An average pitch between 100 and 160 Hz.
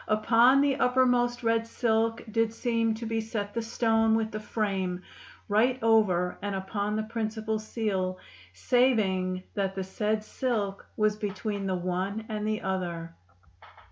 No: high, 215 Hz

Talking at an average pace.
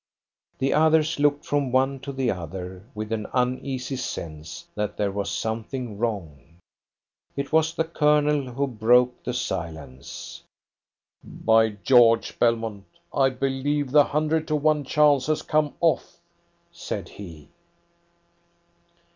No: slow, 125 wpm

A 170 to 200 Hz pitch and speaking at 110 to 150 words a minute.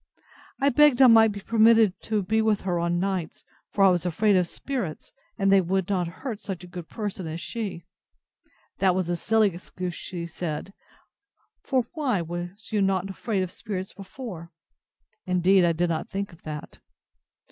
No: high, 190 Hz; average, 175 wpm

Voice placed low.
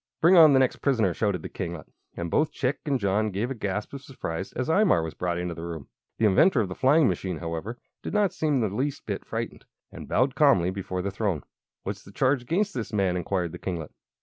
Yes: low, 105 Hz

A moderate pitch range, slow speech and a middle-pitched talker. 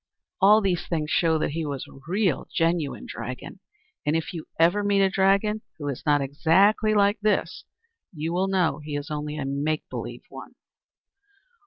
No: average, 4.7 semitones; average, 175 wpm; medium, 165 Hz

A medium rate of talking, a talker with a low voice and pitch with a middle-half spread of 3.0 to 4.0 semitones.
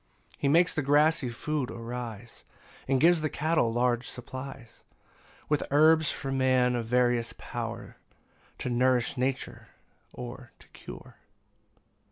No: slow, 130 wpm; low, 130 Hz; average, 3.3 semitones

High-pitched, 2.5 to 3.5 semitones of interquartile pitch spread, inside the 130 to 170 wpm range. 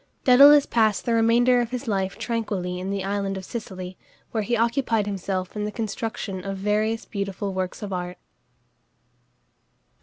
Yes: high, 210 Hz; average, 3.2 semitones; average, 155 wpm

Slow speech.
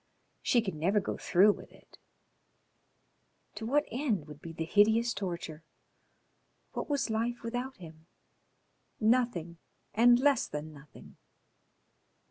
Yes: slow, 120 wpm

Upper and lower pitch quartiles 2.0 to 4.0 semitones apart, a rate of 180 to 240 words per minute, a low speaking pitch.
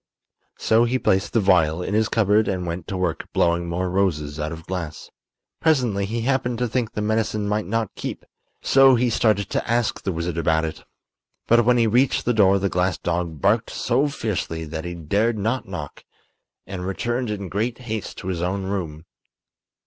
No: average, 4.7 semitones; average, 190 wpm; low, 100 Hz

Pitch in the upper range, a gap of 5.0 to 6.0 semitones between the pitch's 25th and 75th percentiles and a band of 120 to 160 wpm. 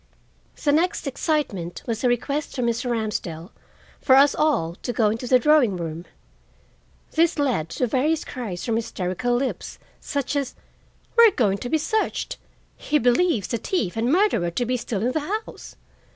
No: high, 245 Hz; wide, 5.4 semitones; average, 170 wpm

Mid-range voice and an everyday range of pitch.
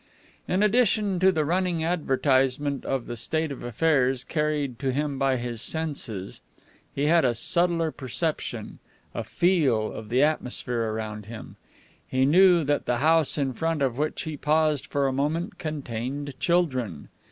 Yes: medium, 145 Hz; average, 4.2 semitones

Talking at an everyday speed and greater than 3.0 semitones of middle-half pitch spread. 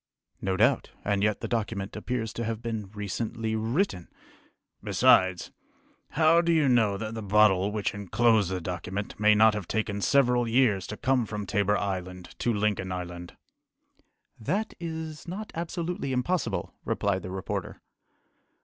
Yes: average, 150 wpm; average, 3.9 semitones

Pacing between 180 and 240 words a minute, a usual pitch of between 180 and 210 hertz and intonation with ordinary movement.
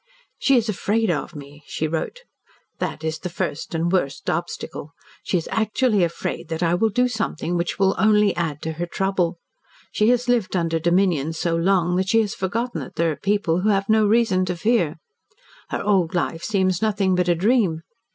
Yes: average, 195 wpm; medium, 185 Hz; average, 4.2 semitones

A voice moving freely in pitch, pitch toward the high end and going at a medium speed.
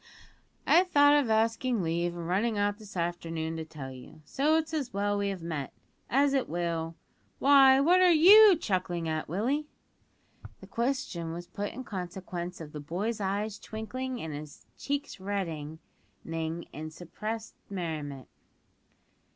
Yes: wide, 7.7 semitones; high, 195 Hz; average, 150 wpm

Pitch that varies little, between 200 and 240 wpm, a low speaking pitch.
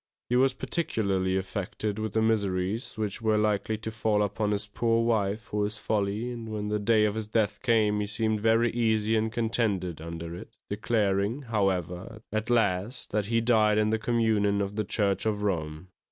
No: narrow, 1.8 semitones; average, 185 wpm; low, 105 Hz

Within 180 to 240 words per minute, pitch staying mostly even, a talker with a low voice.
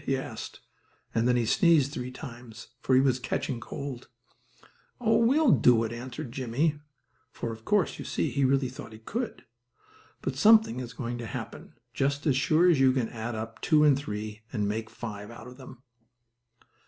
No: average, 190 wpm; average, 3.4 semitones; low, 130 Hz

